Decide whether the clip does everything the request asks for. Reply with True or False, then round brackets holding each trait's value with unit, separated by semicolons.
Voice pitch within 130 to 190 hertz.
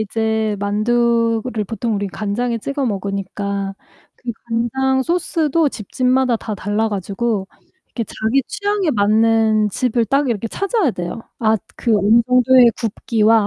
False (225 Hz)